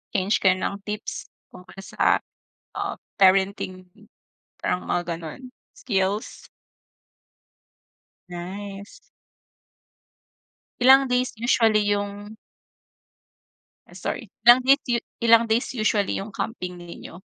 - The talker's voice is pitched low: No, high, 205 Hz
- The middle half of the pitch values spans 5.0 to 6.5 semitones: No, average, 3.5 semitones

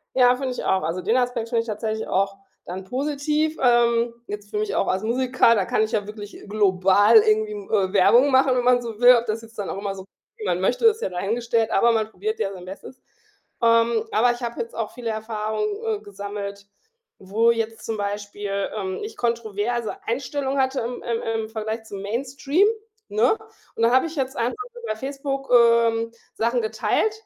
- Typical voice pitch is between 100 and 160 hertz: No, high, 230 Hz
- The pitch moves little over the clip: No, average, 3.4 semitones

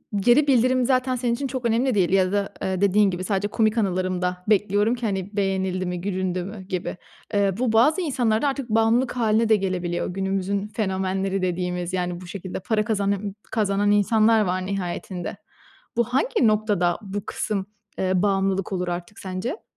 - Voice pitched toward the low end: No, high, 200 Hz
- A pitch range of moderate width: Yes, average, 3.3 semitones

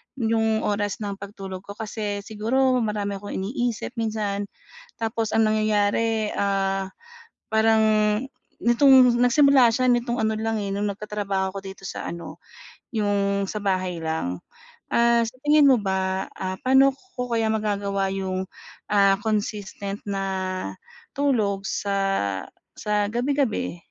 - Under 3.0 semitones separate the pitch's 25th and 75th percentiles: Yes, narrow, 2.4 semitones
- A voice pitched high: Yes, high, 210 Hz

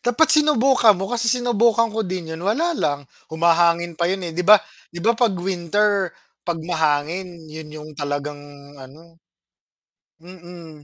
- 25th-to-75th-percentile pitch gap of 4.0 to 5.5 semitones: Yes, average, 4.8 semitones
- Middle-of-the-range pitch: Yes, medium, 175 Hz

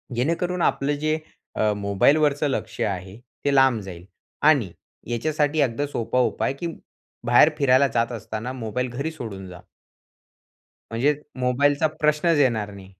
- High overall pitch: No, low, 125 Hz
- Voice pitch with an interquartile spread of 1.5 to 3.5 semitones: No, average, 4.8 semitones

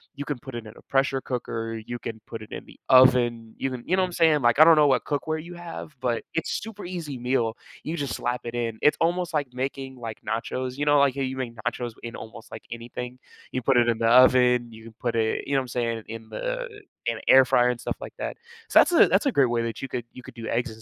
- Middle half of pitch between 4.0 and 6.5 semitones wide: No, average, 3.3 semitones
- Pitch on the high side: No, low, 125 Hz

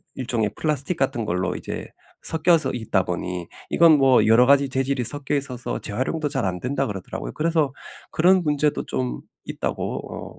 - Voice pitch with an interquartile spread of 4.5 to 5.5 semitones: Yes, average, 5.2 semitones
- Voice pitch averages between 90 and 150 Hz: Yes, low, 135 Hz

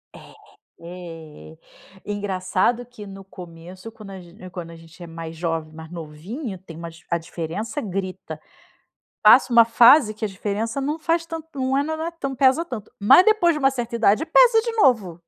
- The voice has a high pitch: Yes, high, 205 Hz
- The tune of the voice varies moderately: No, wide, 7.6 semitones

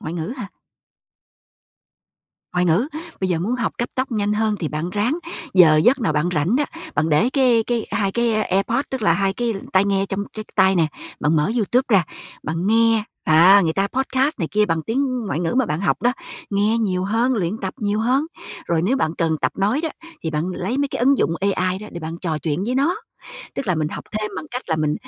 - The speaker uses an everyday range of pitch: No, wide, 5.8 semitones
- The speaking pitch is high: Yes, high, 200 Hz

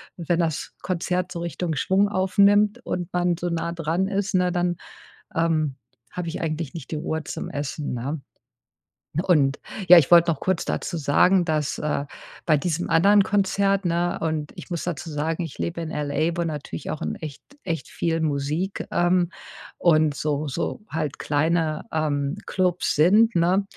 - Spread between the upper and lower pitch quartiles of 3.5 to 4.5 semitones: No, average, 2.8 semitones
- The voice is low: No, medium, 170 Hz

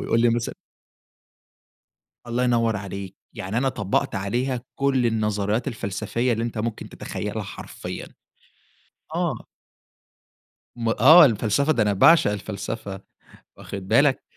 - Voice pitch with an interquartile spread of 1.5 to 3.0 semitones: No, average, 3.4 semitones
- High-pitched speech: No, low, 115 Hz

